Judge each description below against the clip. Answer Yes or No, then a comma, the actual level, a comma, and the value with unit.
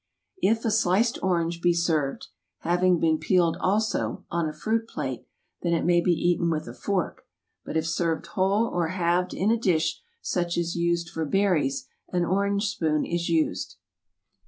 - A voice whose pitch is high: No, medium, 175 Hz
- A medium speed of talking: Yes, average, 170 wpm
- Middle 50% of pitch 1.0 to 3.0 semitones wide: Yes, narrow, 2.5 semitones